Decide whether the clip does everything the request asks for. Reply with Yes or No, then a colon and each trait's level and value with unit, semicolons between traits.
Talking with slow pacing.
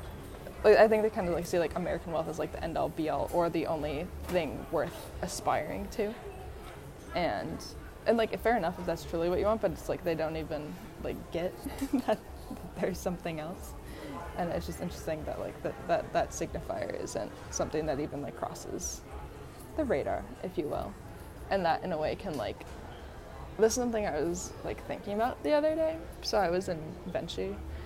No: average, 200 wpm